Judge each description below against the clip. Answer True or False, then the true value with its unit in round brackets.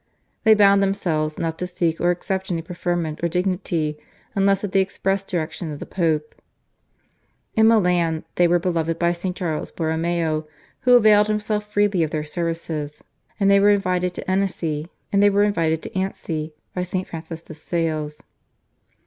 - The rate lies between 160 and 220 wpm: False (150 wpm)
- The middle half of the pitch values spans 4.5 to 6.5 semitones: False (3.4 semitones)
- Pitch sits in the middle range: True (175 Hz)